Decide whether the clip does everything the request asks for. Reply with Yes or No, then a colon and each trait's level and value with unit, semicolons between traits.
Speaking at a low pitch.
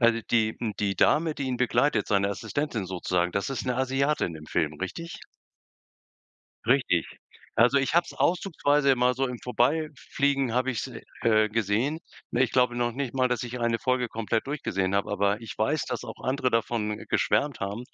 Yes: low, 120 Hz